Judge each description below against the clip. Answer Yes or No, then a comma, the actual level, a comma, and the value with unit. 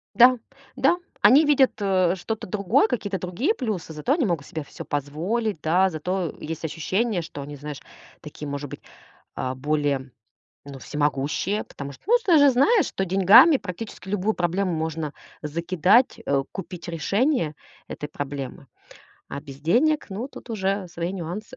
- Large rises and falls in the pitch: Yes, wide, 6.6 semitones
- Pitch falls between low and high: Yes, medium, 180 Hz